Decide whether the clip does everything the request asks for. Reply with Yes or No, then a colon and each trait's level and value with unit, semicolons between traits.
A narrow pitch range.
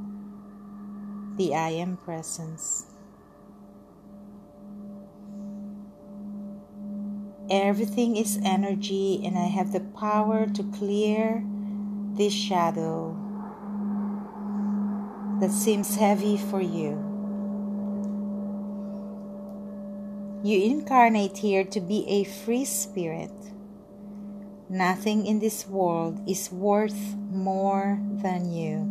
Yes: narrow, 0.8 semitones